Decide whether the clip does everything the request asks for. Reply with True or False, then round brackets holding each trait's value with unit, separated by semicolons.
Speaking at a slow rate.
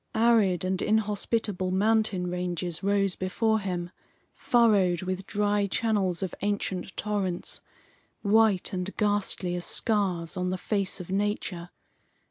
True (120 wpm)